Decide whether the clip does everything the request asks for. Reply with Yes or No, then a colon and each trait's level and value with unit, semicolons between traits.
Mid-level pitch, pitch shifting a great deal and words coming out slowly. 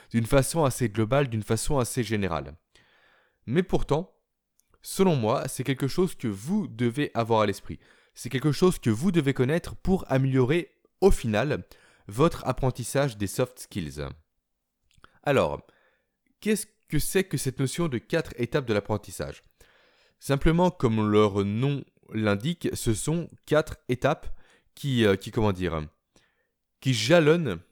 No: low, 130 Hz; wide, 6.9 semitones; slow, 140 wpm